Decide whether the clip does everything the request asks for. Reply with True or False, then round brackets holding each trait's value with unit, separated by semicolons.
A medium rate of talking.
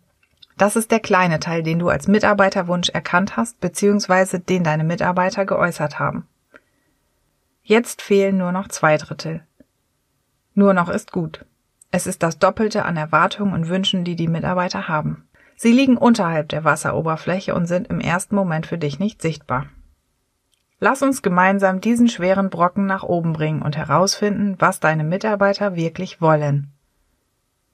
True (150 wpm)